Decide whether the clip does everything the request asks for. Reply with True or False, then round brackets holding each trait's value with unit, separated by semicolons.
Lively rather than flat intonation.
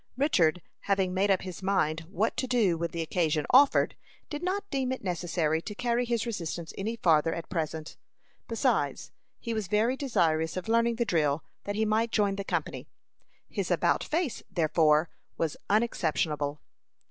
True (6.2 semitones)